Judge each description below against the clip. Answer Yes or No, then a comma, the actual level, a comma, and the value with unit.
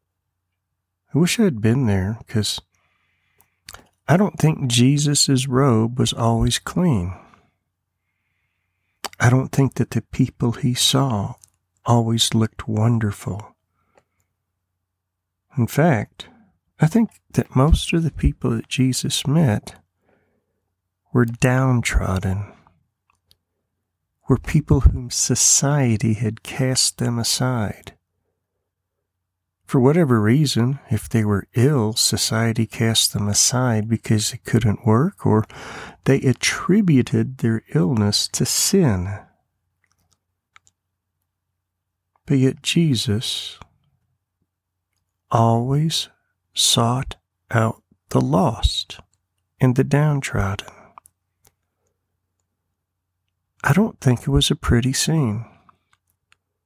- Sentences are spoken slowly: Yes, slow, 95 wpm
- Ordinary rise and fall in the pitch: No, wide, 5.8 semitones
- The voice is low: Yes, low, 110 Hz